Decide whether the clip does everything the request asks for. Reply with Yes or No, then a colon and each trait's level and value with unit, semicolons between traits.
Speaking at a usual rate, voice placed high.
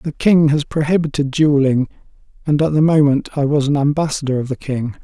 No: average, 190 wpm; medium, 145 Hz